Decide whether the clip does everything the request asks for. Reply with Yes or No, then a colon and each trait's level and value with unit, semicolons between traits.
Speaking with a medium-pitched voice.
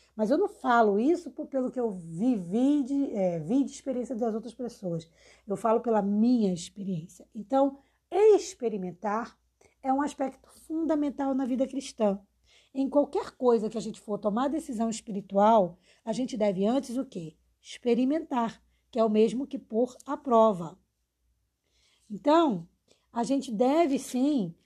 No: high, 235 Hz